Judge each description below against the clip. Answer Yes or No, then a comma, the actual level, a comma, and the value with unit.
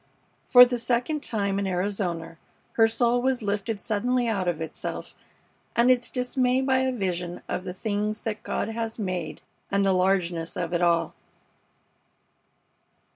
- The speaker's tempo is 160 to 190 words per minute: No, average, 150 wpm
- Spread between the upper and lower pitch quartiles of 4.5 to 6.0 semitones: Yes, average, 5.0 semitones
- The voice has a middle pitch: No, high, 210 Hz